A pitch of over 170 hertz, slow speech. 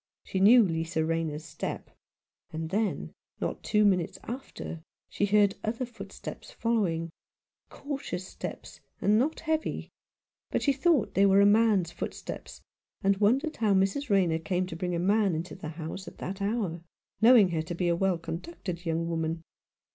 No: high, 190 Hz; average, 165 wpm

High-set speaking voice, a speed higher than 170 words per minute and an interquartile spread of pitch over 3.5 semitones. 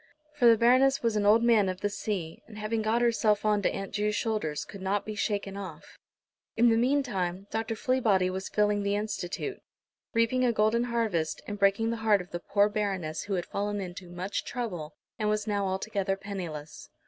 No: high, 210 Hz; average, 195 wpm; average, 2.8 semitones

